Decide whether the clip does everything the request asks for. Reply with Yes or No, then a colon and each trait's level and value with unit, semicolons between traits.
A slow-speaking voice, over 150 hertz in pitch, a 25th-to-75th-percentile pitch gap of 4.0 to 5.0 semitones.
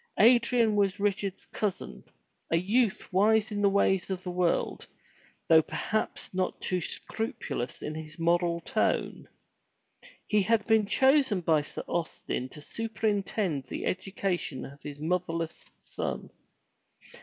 Yes: slow, 130 wpm; high, 190 Hz; average, 4.3 semitones